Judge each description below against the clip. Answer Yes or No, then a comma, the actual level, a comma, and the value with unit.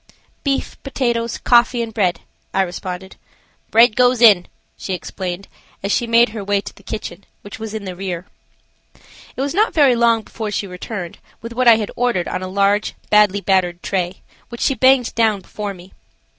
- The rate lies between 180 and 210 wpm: Yes, average, 185 wpm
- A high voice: Yes, high, 210 Hz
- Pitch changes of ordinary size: Yes, average, 3.7 semitones